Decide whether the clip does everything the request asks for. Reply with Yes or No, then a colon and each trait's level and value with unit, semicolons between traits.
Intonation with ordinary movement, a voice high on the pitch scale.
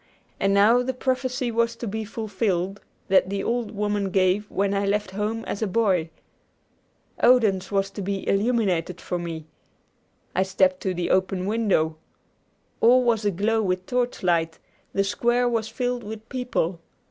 Yes: average, 3.5 semitones; high, 205 Hz